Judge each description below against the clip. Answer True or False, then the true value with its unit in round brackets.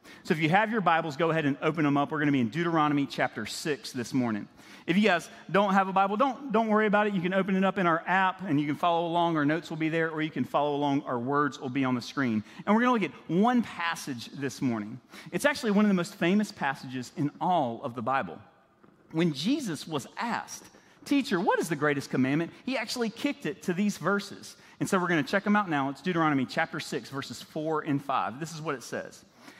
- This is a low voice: False (165 Hz)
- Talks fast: True (255 wpm)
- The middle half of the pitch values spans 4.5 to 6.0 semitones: True (5.5 semitones)